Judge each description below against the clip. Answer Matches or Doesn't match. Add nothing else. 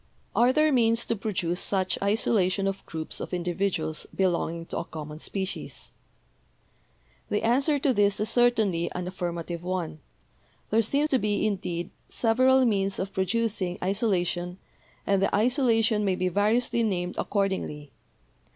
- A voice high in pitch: Matches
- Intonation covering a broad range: Doesn't match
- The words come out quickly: Doesn't match